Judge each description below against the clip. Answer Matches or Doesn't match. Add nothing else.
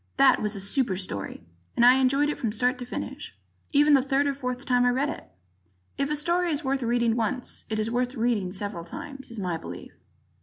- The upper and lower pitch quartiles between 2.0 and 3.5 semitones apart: Doesn't match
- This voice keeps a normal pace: Doesn't match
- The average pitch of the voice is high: Matches